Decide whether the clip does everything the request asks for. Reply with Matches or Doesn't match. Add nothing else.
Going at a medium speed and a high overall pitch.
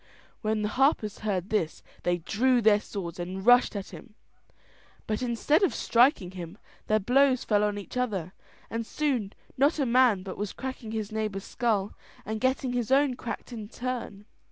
Matches